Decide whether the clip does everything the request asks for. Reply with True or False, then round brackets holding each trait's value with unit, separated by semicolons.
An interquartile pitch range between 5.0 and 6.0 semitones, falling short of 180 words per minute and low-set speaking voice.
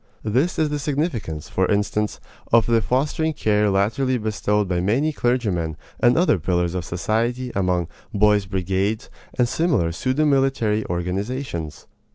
True (5.5 semitones; 140 wpm; 105 Hz)